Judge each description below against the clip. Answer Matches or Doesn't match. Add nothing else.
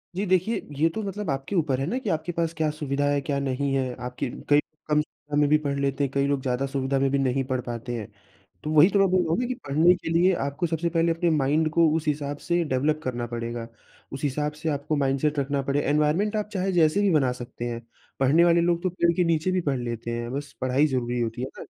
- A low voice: Doesn't match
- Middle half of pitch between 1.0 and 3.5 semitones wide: Doesn't match